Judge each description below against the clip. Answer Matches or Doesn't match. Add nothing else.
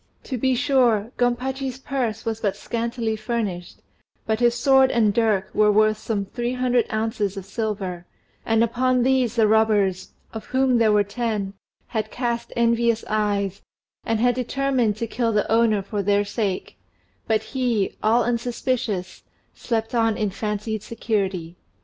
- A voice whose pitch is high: Matches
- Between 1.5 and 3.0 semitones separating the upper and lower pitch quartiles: Matches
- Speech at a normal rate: Matches